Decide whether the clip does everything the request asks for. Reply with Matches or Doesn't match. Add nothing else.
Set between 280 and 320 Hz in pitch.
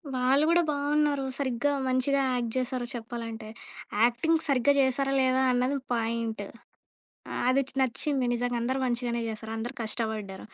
Doesn't match